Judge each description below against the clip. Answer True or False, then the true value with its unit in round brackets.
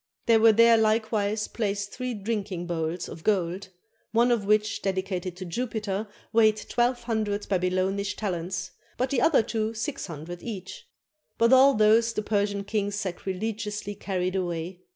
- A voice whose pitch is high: True (205 Hz)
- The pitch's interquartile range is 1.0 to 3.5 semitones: True (3.1 semitones)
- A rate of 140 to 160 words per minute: True (150 wpm)